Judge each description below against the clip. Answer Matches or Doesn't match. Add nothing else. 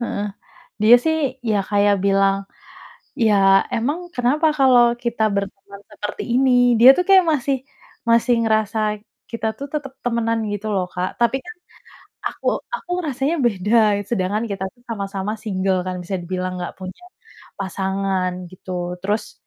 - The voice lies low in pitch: Doesn't match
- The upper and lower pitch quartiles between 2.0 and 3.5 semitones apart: Doesn't match